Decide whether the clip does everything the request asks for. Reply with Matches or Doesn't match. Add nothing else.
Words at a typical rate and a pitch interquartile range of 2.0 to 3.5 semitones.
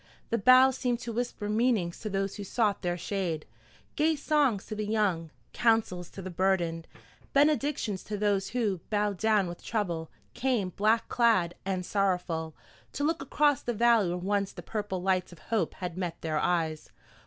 Doesn't match